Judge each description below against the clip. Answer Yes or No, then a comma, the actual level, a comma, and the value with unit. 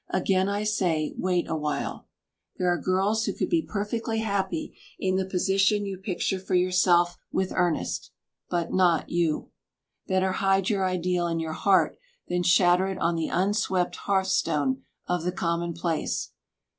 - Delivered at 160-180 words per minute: No, average, 150 wpm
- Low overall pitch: No, medium, 185 Hz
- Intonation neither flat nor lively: No, narrow, 2.0 semitones